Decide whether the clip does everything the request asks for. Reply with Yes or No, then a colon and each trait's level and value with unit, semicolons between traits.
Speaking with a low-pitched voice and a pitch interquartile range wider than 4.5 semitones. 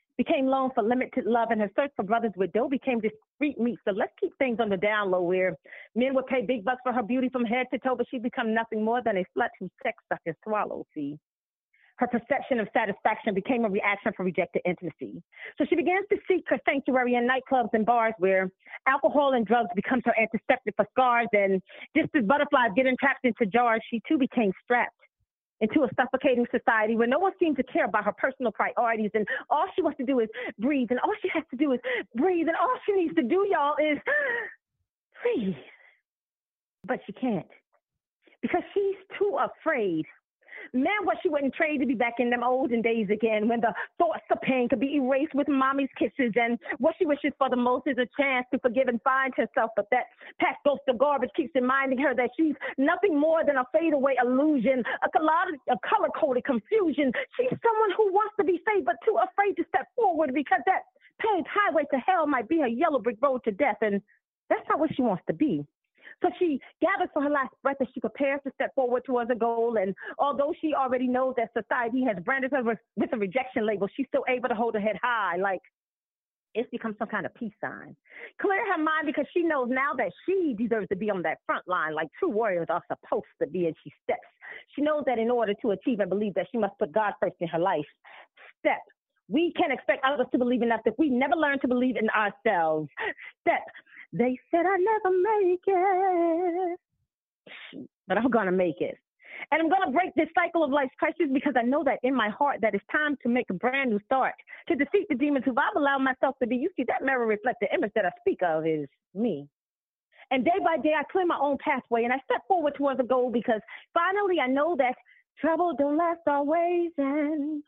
No: very high, 265 Hz; average, 5.2 semitones